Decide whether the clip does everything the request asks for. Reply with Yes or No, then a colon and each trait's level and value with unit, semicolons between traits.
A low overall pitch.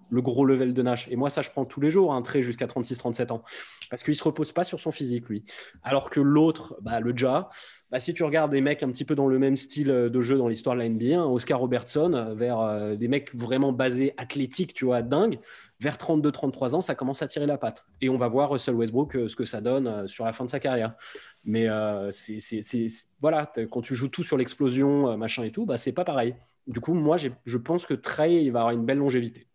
Yes: low, 130 Hz